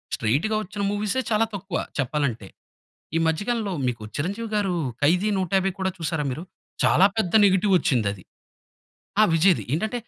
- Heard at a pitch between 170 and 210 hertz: Yes, medium, 185 Hz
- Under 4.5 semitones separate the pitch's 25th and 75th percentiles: No, wide, 5.6 semitones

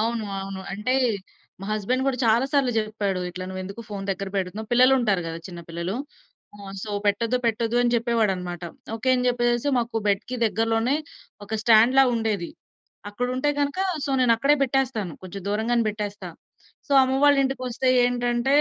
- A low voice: No, high, 225 Hz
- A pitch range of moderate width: Yes, average, 3.7 semitones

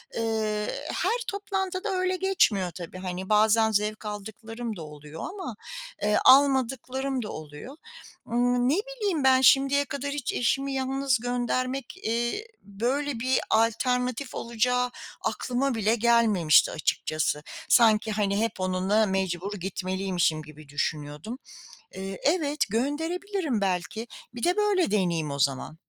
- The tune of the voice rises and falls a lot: Yes, wide, 6.0 semitones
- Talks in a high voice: Yes, high, 230 Hz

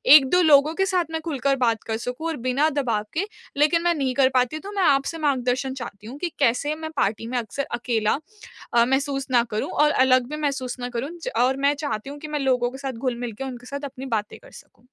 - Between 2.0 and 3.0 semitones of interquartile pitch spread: No, average, 3.5 semitones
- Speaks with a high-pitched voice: Yes, very high, 270 Hz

